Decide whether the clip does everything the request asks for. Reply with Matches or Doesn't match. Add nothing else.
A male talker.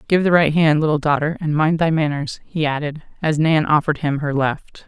Doesn't match